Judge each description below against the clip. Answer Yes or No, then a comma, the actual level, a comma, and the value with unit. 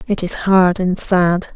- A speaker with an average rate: Yes, average, 190 wpm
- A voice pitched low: No, medium, 185 Hz